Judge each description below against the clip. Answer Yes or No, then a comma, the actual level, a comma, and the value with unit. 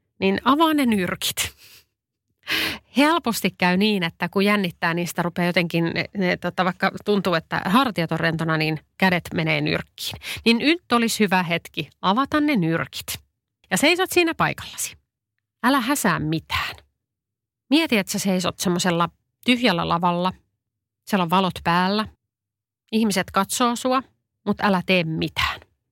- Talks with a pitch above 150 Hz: Yes, medium, 185 Hz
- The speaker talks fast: No, average, 135 wpm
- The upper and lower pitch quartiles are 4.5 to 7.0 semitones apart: Yes, average, 4.8 semitones